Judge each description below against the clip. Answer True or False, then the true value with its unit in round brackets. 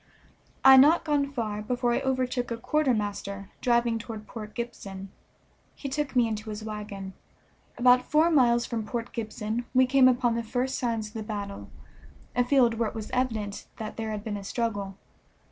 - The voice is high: True (230 Hz)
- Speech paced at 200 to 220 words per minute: False (180 wpm)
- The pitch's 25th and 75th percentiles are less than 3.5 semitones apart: True (3.0 semitones)